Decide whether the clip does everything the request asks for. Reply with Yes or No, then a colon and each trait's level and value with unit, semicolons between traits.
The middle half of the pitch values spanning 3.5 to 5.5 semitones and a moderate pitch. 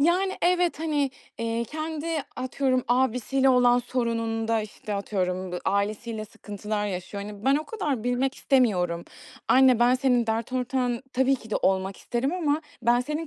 No: average, 3.9 semitones; high, 245 Hz